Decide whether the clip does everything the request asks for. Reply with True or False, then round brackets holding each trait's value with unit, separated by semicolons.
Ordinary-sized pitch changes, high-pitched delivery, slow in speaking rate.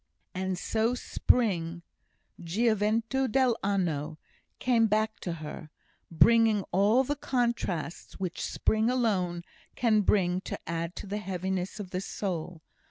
True (4.4 semitones; 200 Hz; 120 wpm)